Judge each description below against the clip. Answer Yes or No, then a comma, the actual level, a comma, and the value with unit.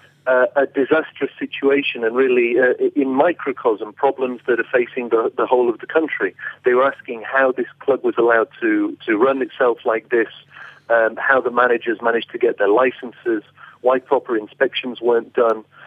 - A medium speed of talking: Yes, average, 180 wpm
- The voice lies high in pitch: Yes, very high, 305 Hz